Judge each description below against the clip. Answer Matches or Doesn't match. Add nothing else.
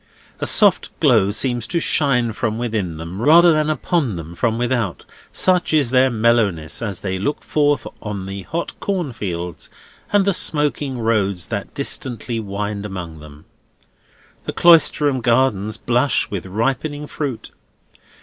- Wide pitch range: Matches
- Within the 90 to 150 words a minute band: Matches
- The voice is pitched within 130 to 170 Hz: Doesn't match